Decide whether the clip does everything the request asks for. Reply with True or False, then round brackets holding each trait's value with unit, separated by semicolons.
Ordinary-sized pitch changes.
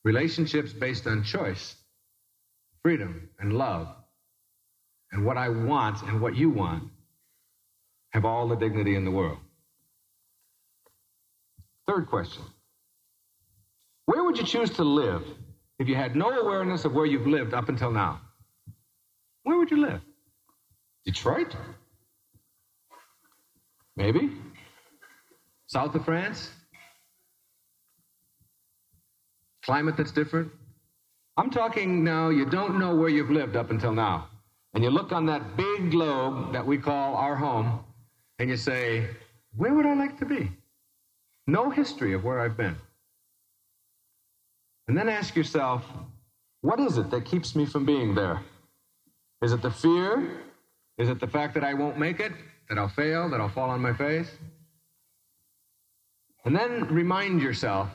False (6.6 semitones)